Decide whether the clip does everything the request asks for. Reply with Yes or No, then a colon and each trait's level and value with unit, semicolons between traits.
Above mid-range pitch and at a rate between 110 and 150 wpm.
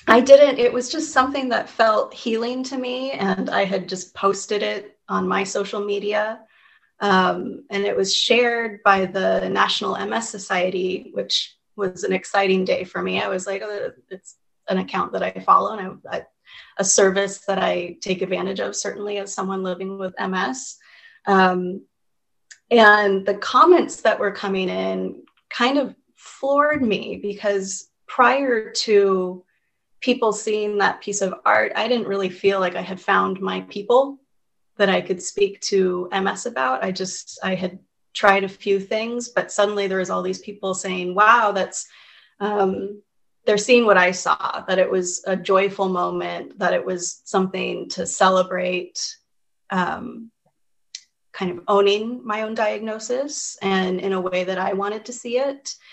No: high, 200 Hz; average, 165 wpm